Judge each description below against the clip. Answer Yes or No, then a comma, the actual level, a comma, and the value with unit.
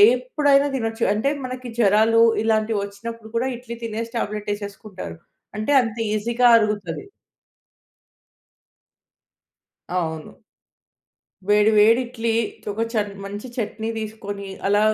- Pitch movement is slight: Yes, narrow, 2.0 semitones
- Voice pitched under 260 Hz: Yes, high, 220 Hz